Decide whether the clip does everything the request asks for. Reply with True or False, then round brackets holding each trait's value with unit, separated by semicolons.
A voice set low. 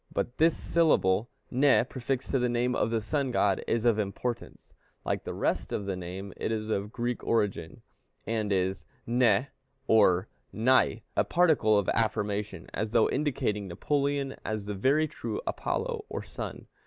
True (115 Hz)